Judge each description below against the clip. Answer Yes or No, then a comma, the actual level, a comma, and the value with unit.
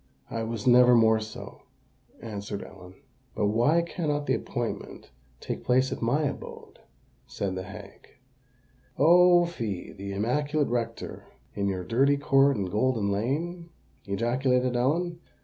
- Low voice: Yes, low, 120 Hz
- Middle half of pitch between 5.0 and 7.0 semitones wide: Yes, wide, 5.4 semitones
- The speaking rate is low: Yes, slow, 130 wpm